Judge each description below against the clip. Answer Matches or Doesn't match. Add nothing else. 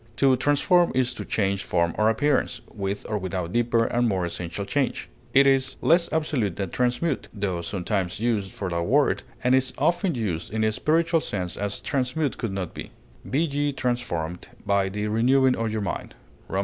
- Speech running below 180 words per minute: Doesn't match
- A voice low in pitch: Matches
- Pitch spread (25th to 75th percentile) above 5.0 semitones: Matches